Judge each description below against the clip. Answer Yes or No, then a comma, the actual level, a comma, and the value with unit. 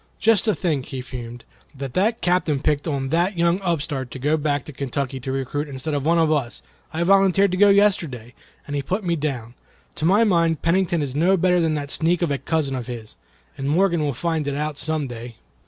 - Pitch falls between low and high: Yes, medium, 150 Hz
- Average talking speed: No, fast, 220 wpm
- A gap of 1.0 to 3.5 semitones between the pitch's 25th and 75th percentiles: No, average, 4.3 semitones